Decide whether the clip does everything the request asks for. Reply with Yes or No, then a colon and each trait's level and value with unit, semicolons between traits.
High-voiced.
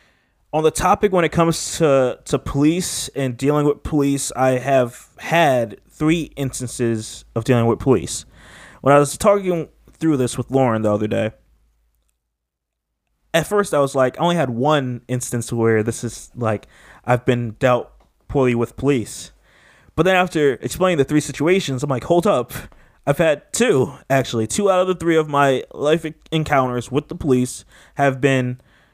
No: low, 135 Hz